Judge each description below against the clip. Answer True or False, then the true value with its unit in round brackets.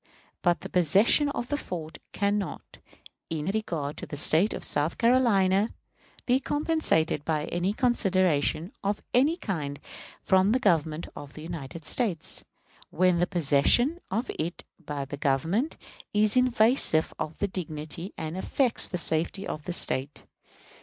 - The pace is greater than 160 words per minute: False (145 wpm)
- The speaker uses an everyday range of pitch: False (5.9 semitones)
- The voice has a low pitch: False (180 Hz)